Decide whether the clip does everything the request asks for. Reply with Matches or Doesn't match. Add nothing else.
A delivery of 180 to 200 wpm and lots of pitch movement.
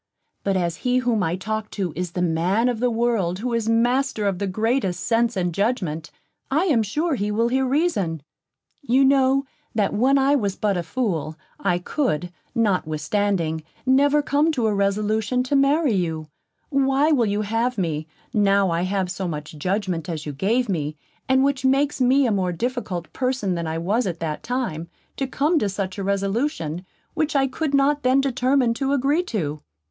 Matches